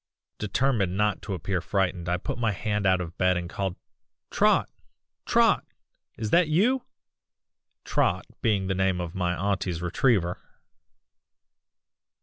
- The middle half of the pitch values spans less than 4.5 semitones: Yes, average, 3.0 semitones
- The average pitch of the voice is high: No, very low, 95 Hz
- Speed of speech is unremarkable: No, slow, 130 wpm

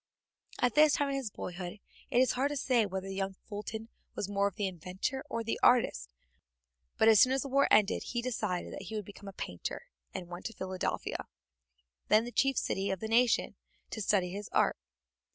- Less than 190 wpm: No, fast, 205 wpm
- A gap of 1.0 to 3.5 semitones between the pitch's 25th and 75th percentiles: No, average, 4.3 semitones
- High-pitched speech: Yes, high, 210 Hz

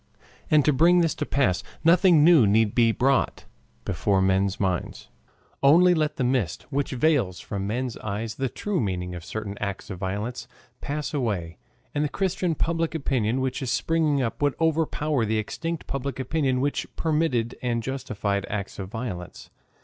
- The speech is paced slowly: No, average, 165 wpm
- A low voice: Yes, low, 130 Hz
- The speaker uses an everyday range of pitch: No, wide, 6.7 semitones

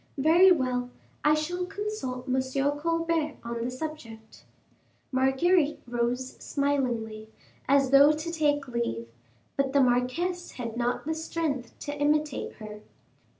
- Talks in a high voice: Yes, very high, 275 Hz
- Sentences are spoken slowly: Yes, slow, 125 wpm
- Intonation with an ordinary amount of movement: Yes, average, 4.2 semitones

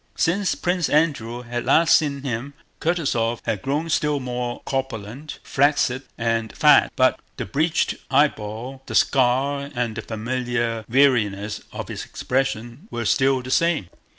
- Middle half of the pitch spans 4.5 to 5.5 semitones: No, average, 3.7 semitones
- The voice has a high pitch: No, low, 130 Hz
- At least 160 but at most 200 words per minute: No, average, 140 wpm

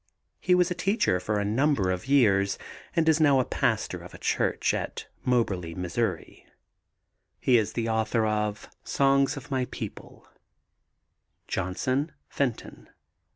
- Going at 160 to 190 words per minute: No, average, 140 wpm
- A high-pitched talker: No, low, 120 Hz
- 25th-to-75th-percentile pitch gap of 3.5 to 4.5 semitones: No, wide, 5.5 semitones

